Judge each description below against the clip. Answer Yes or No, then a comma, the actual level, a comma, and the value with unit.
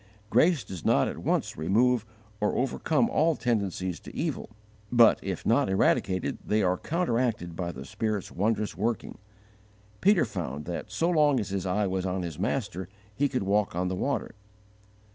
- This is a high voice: No, low, 105 Hz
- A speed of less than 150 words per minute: No, average, 165 wpm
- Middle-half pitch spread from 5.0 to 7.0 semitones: Yes, wide, 5.5 semitones